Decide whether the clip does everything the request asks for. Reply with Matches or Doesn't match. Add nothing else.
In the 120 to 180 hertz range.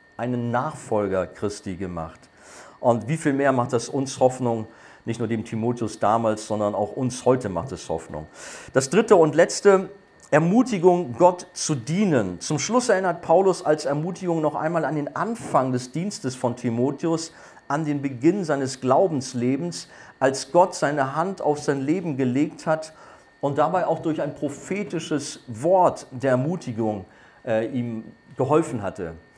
Matches